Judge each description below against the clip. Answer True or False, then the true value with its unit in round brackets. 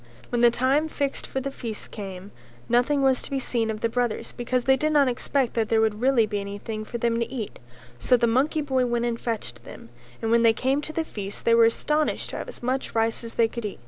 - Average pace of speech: False (250 wpm)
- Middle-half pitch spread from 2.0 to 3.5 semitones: True (2.9 semitones)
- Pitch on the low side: False (235 Hz)